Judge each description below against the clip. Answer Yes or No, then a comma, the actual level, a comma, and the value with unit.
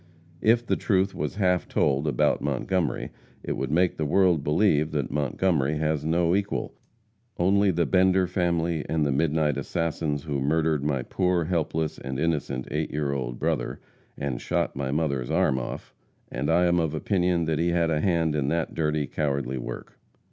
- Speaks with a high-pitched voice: No, very low, 80 Hz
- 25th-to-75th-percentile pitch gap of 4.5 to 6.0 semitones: No, average, 3.4 semitones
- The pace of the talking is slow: No, average, 170 wpm